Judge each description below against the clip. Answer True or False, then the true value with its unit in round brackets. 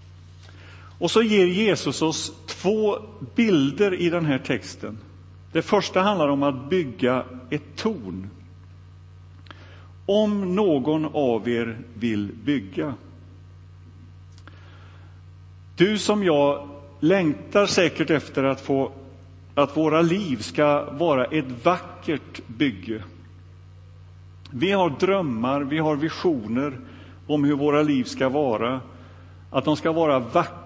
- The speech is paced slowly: True (115 wpm)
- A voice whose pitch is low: True (130 Hz)